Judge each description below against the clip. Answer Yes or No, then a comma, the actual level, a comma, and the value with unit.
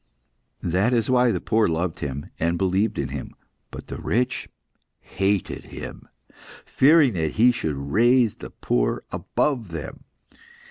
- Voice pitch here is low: Yes, low, 100 Hz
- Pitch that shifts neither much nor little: No, wide, 6.9 semitones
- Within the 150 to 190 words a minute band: No, average, 140 wpm